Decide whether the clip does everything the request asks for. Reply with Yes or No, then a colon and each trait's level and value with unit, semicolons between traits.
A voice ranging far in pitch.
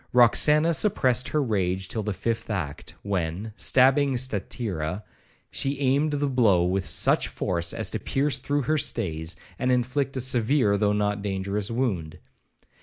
Yes: wide, 5.7 semitones